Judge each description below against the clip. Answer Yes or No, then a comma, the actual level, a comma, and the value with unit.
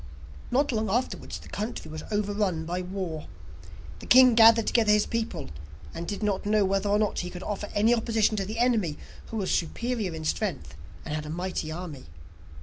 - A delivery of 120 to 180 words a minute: No, average, 190 wpm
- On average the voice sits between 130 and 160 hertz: No, high, 205 Hz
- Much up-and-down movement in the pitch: No, average, 4.1 semitones